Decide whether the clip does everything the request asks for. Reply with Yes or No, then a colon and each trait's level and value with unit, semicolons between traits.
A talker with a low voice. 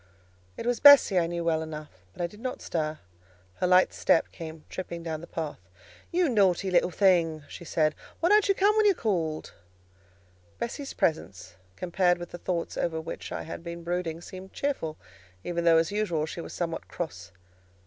No: medium, 170 Hz